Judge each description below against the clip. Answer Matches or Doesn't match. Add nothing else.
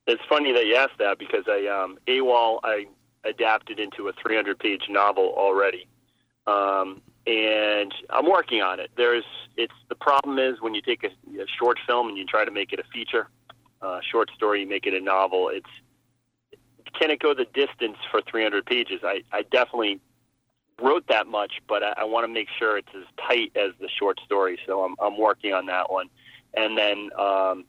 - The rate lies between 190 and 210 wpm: Matches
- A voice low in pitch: Matches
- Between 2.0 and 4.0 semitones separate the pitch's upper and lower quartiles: Doesn't match